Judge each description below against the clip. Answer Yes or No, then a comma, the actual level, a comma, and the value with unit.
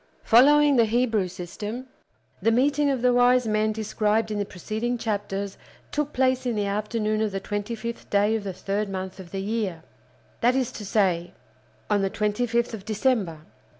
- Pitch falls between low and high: No, high, 215 Hz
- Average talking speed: Yes, average, 185 wpm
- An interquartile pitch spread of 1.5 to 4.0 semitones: Yes, average, 3.3 semitones